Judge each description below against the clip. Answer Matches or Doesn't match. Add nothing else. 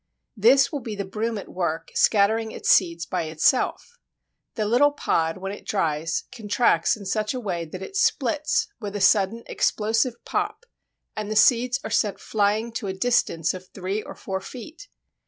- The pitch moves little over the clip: Doesn't match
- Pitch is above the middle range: Matches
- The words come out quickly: Doesn't match